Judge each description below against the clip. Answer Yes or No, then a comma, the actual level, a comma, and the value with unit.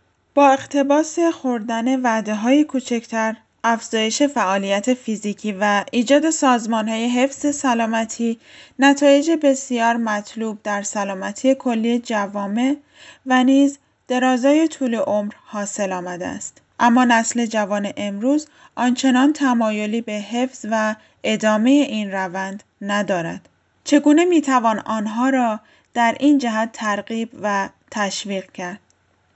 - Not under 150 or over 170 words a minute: No, average, 110 wpm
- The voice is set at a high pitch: Yes, high, 230 Hz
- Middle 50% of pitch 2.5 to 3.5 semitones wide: No, average, 4.2 semitones